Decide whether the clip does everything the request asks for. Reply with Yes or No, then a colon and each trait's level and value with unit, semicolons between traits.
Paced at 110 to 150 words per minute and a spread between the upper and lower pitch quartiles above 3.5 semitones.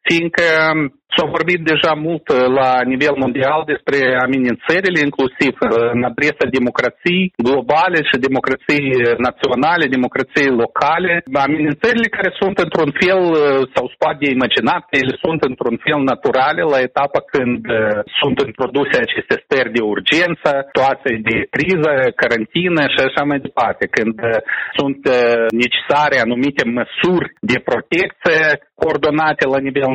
Yes: average, 120 wpm; average, 4.3 semitones